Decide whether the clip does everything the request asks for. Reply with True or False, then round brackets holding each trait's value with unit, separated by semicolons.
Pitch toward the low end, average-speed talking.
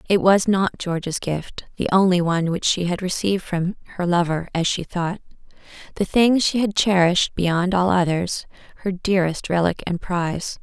False (180 Hz; 165 wpm)